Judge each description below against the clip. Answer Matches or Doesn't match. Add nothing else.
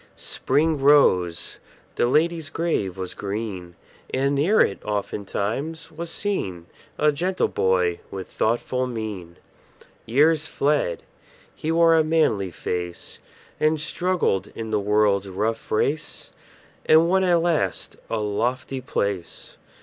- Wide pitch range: Matches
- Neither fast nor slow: Doesn't match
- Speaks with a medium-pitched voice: Doesn't match